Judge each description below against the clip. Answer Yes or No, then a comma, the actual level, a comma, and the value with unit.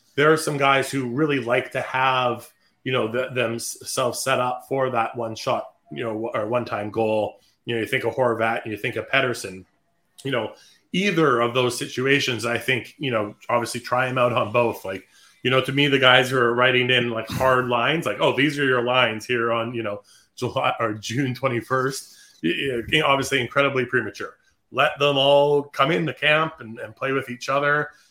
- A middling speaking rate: No, fast, 210 wpm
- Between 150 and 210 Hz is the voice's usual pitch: No, low, 125 Hz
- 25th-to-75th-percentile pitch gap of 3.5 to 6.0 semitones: No, narrow, 2.6 semitones